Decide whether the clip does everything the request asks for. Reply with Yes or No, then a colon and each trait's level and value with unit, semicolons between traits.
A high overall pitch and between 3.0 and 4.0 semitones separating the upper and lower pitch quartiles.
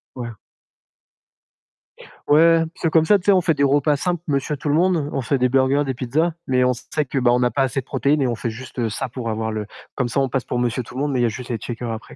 No: low, 130 Hz; average, 3.3 semitones